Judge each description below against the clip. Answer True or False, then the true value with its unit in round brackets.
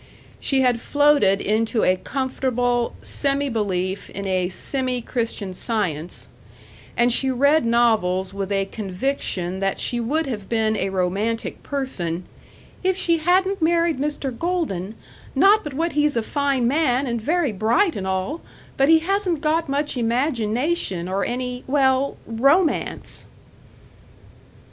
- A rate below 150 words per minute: True (135 wpm)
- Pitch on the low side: False (245 Hz)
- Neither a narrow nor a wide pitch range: False (6.5 semitones)